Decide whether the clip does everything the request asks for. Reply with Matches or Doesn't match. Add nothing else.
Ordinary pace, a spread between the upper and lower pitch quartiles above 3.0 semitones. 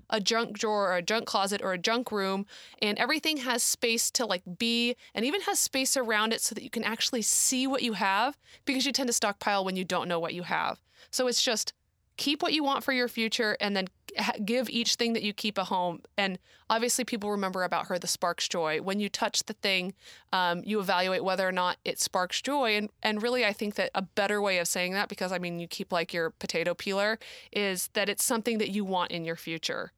Doesn't match